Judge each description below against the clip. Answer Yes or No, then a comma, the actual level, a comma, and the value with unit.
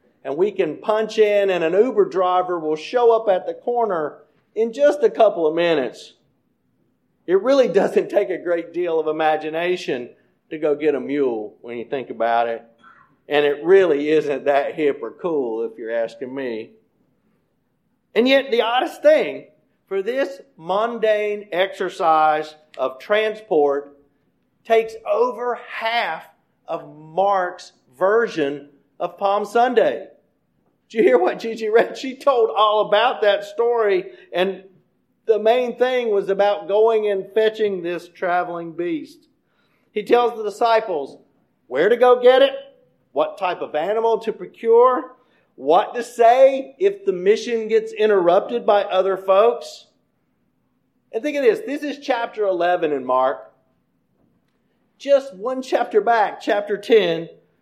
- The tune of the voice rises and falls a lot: Yes, wide, 6.2 semitones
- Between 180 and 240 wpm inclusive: No, average, 145 wpm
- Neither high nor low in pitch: No, high, 210 Hz